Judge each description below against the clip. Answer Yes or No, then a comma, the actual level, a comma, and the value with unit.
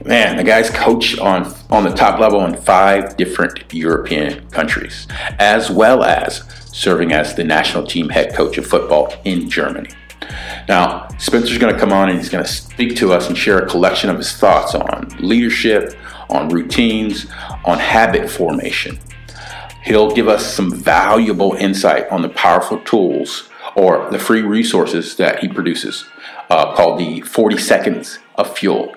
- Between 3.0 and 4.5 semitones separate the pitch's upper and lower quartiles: No, narrow, 2.6 semitones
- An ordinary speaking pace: Yes, average, 165 wpm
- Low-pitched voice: Yes, low, 105 Hz